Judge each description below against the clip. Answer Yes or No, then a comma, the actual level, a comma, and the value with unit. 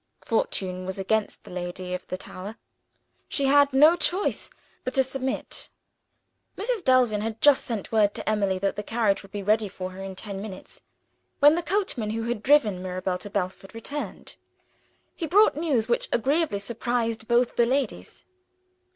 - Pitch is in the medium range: No, high, 225 Hz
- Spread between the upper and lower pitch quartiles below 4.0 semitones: No, wide, 5.5 semitones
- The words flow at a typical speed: Yes, average, 170 wpm